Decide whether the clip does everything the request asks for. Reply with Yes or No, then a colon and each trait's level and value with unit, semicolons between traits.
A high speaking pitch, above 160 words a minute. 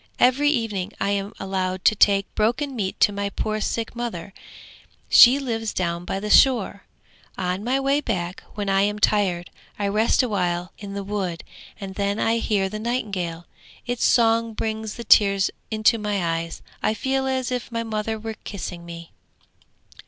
Yes: high, 210 Hz; average, 170 wpm